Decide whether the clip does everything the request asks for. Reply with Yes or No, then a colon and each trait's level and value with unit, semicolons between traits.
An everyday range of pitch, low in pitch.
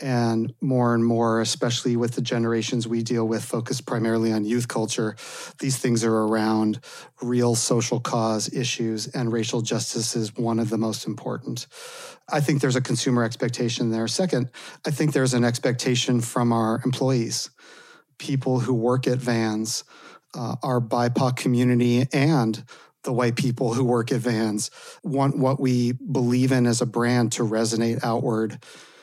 No: narrow, 2.0 semitones; low, 120 Hz